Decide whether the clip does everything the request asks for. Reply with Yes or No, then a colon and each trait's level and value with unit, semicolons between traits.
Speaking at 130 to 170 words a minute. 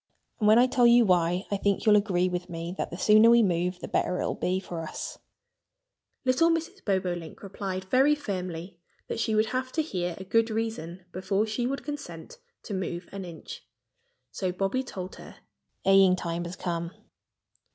No: average, 185 wpm